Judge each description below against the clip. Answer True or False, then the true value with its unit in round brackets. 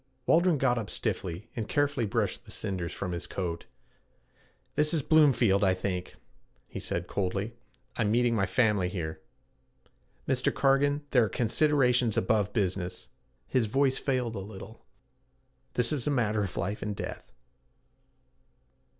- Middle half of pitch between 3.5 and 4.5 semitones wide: False (5.3 semitones)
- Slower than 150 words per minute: True (140 wpm)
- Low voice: True (110 Hz)